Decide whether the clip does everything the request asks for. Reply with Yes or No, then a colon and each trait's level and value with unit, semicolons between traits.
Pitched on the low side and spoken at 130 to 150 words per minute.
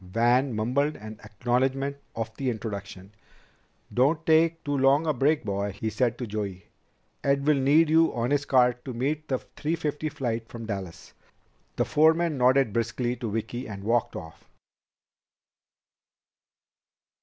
Yes: low, 125 Hz; average, 145 wpm